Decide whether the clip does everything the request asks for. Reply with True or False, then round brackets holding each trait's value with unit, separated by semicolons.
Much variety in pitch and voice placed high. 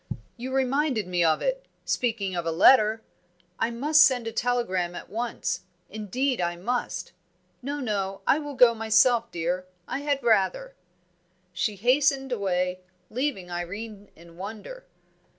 True (5.8 semitones; 225 Hz)